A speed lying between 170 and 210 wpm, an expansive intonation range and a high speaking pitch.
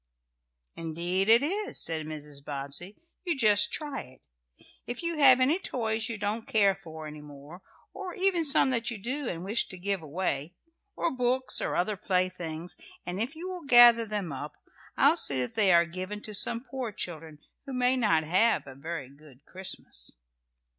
Yes: average, 180 wpm; wide, 7.5 semitones; high, 200 Hz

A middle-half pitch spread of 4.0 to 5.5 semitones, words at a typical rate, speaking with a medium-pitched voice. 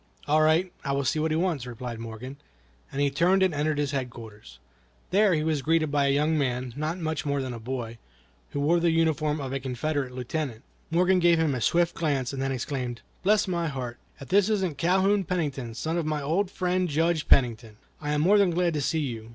No: average, 4.5 semitones; fast, 220 wpm; medium, 150 Hz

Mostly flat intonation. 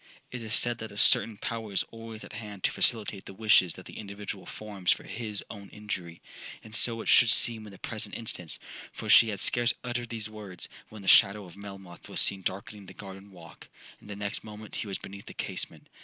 Yes: narrow, 2.2 semitones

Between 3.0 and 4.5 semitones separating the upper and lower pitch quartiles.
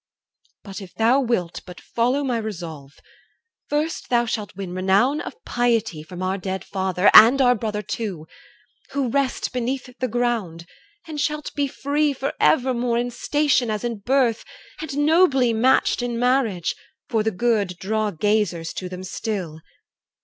No: average, 5.2 semitones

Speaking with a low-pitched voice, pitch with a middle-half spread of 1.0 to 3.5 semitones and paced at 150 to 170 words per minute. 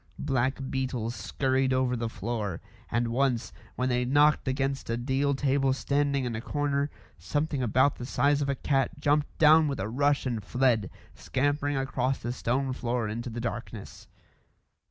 Yes: low, 130 Hz; average, 2.8 semitones; average, 165 wpm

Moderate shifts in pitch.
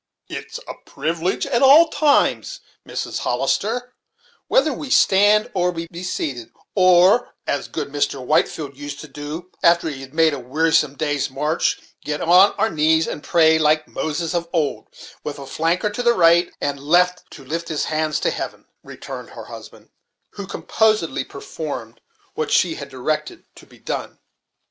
Yes: average, 3.8 semitones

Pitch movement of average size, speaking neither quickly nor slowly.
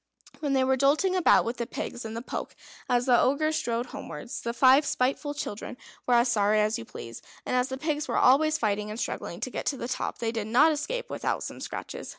No: average, 4.0 semitones; fast, 230 wpm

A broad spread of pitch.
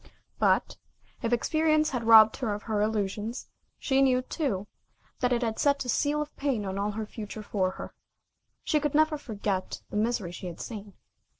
No: average, 4.9 semitones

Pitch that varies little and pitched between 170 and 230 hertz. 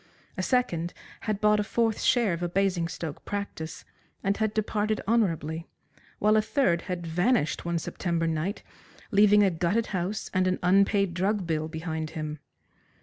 No: average, 4.0 semitones; medium, 185 Hz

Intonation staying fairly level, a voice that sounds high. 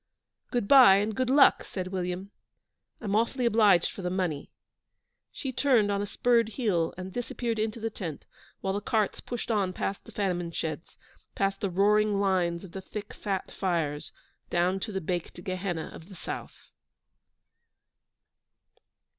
No: average, 3.2 semitones; high, 195 Hz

